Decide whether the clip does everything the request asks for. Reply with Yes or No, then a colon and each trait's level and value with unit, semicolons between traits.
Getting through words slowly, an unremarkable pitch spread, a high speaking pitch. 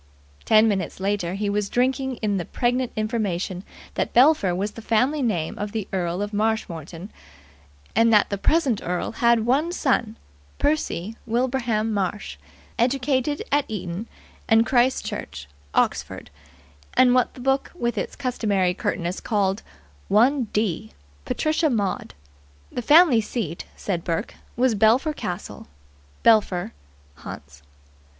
Yes: slow, 130 wpm; average, 4.6 semitones; high, 220 Hz